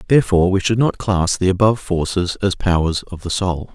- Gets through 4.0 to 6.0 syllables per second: Yes, 5.6 syllables/s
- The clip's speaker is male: Yes, male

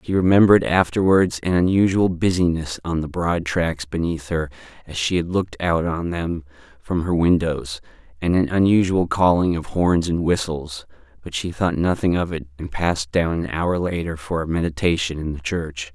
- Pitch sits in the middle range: No, very low, 85 Hz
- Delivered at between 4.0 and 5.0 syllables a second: Yes, 4.9 syllables/s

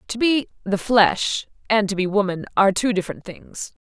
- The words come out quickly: No, average, 190 wpm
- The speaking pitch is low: No, high, 205 Hz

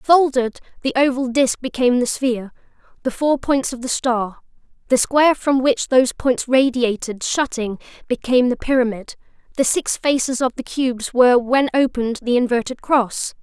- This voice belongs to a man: No, female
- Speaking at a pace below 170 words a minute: Yes, average, 160 wpm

